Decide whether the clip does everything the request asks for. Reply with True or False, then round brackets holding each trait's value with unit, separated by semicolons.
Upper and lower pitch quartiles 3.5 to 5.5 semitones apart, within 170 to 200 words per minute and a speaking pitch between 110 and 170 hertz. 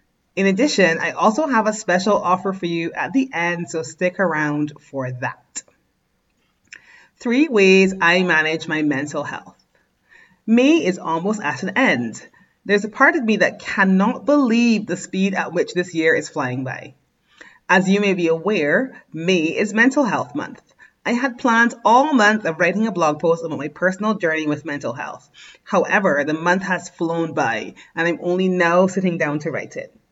False (4.9 semitones; 180 wpm; 180 Hz)